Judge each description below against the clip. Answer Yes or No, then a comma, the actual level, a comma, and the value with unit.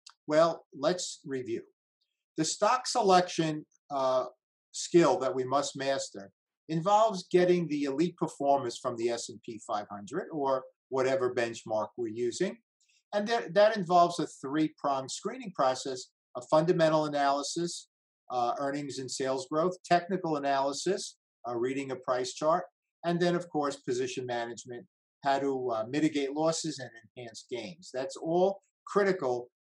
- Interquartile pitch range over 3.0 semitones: Yes, wide, 5.5 semitones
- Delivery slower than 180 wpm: Yes, slow, 135 wpm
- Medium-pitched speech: Yes, medium, 155 Hz